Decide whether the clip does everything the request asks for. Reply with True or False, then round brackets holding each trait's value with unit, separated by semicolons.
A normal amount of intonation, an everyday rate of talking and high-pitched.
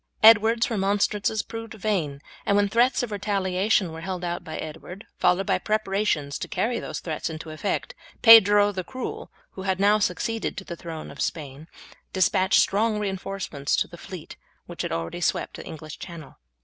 True (4.3 semitones; 175 wpm; 195 Hz)